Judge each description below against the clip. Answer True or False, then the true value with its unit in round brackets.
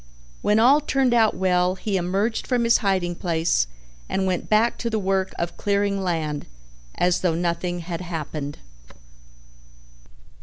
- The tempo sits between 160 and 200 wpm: False (145 wpm)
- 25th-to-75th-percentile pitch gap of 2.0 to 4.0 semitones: True (3.7 semitones)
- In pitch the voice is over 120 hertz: True (185 Hz)